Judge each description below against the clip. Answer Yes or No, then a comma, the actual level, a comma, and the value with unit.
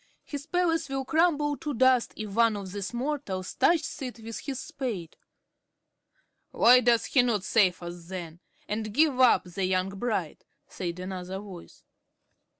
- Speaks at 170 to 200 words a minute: No, average, 150 wpm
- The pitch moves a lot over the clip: Yes, wide, 6.2 semitones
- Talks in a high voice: Yes, high, 225 Hz